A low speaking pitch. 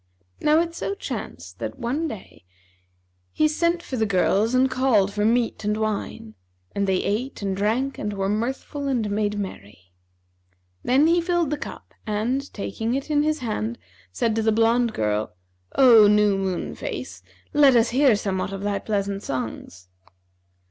No: high, 220 Hz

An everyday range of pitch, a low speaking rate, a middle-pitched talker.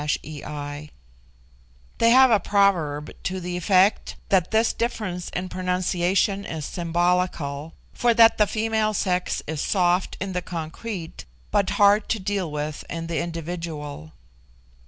Yes: average, 3.4 semitones; slow, 130 wpm; medium, 180 Hz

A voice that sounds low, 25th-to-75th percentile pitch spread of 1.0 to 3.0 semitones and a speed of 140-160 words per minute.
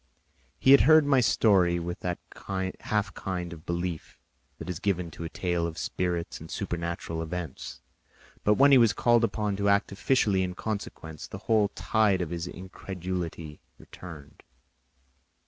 No: very low, 90 Hz; average, 3.6 semitones; average, 155 wpm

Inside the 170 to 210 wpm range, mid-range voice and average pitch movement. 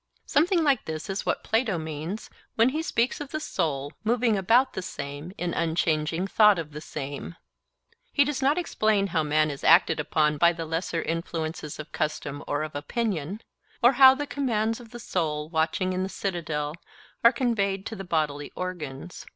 No: average, 180 wpm; medium, 175 Hz; wide, 6.6 semitones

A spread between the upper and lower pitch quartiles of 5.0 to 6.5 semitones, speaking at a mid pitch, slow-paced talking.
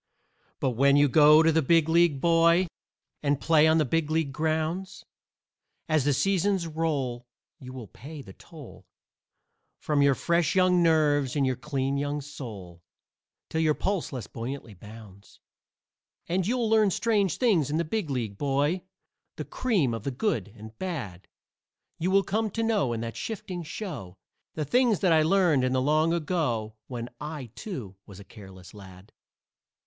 No: average, 5.3 semitones; medium, 150 Hz; average, 165 wpm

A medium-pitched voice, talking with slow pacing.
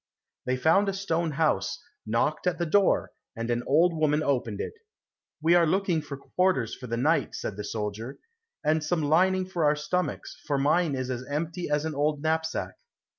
No: medium, 155 Hz; average, 185 wpm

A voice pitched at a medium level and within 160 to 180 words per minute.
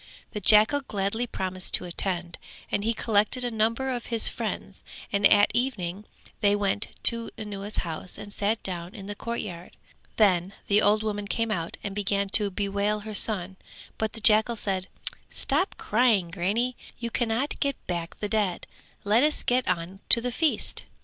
No: high, 210 Hz; average, 170 wpm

